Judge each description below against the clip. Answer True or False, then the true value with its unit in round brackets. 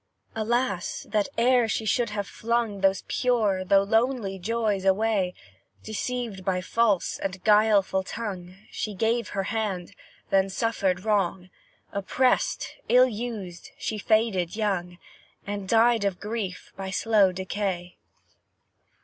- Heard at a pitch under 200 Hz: False (205 Hz)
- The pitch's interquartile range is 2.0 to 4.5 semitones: True (2.9 semitones)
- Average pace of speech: False (125 wpm)